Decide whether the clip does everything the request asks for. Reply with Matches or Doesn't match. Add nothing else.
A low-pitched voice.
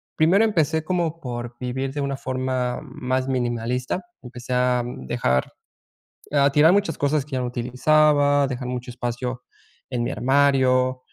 Matches